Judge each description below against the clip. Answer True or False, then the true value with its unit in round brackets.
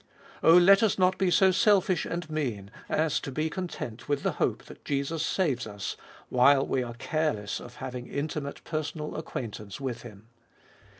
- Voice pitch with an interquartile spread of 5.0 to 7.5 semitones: True (5.4 semitones)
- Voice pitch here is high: False (145 Hz)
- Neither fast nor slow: True (170 wpm)